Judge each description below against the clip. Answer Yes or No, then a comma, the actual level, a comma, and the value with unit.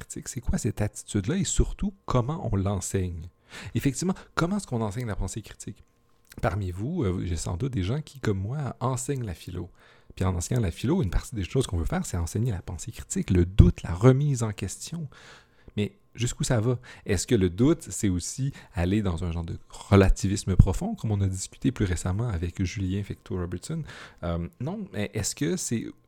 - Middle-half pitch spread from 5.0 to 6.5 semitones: Yes, average, 5.3 semitones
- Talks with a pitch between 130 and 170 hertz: No, low, 105 Hz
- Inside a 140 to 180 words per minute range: No, average, 200 wpm